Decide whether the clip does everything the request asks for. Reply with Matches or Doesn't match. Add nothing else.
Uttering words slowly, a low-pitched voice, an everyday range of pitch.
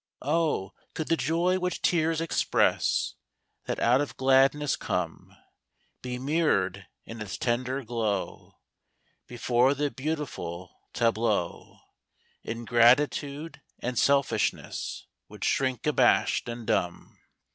Matches